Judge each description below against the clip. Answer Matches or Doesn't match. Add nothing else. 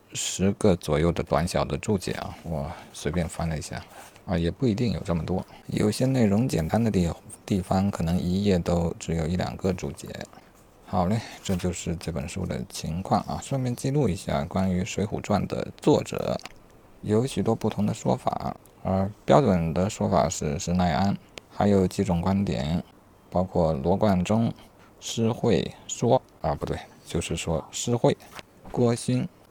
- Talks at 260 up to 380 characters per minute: Doesn't match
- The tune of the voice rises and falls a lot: Doesn't match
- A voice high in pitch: Doesn't match